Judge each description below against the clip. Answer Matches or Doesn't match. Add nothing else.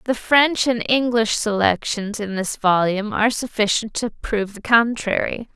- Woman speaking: Matches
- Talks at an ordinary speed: Matches